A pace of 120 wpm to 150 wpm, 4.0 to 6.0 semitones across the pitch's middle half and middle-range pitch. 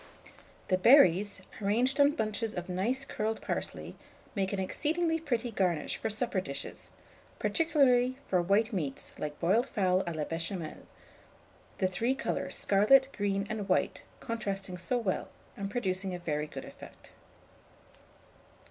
No: average, 140 wpm; average, 4.8 semitones; high, 200 Hz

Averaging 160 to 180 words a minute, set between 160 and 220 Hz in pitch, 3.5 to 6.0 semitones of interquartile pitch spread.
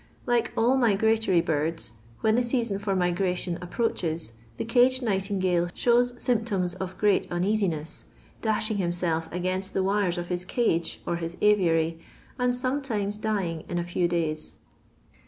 No: average, 145 wpm; high, 190 Hz; average, 4.2 semitones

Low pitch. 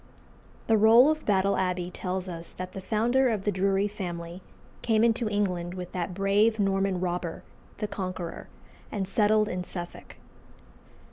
No: high, 195 Hz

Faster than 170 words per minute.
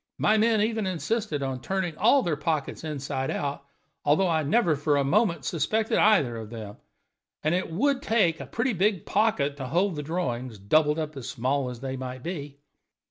Yes: average, 190 wpm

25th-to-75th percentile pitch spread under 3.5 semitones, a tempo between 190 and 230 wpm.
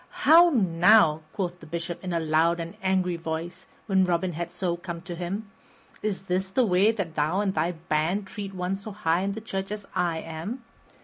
Yes: average, 2.8 semitones; average, 200 wpm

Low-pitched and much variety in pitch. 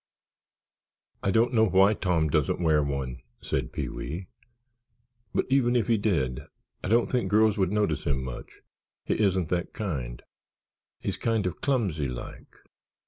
Yes: very low, 90 Hz; wide, 7.0 semitones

